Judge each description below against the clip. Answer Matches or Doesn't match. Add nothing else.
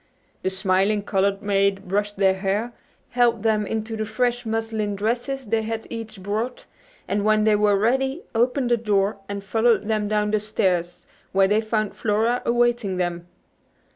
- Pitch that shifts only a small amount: Matches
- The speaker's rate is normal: Matches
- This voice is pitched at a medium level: Doesn't match